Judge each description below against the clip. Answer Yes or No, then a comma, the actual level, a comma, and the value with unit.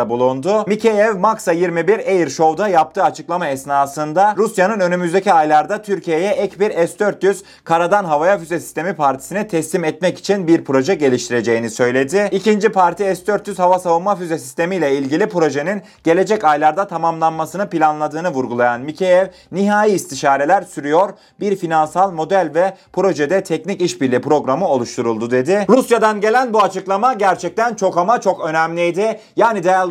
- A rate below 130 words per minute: No, average, 135 wpm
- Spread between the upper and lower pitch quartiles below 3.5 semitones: No, average, 4.4 semitones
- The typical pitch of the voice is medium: Yes, medium, 180 Hz